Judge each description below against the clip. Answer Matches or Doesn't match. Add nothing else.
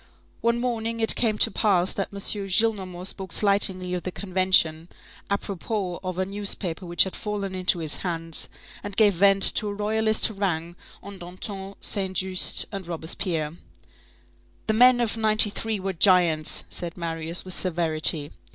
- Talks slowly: Doesn't match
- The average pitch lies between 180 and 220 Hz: Matches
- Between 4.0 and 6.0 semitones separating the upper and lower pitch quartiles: Doesn't match